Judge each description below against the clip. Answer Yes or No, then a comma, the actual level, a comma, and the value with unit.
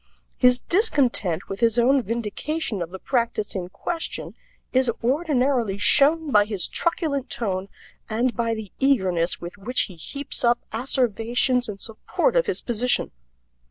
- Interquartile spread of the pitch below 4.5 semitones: No, average, 4.9 semitones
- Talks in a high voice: Yes, high, 235 Hz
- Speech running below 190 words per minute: Yes, average, 145 wpm